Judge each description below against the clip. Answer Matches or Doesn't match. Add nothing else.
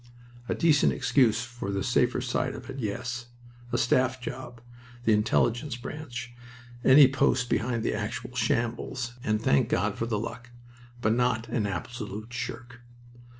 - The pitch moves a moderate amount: Doesn't match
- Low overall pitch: Matches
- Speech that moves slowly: Doesn't match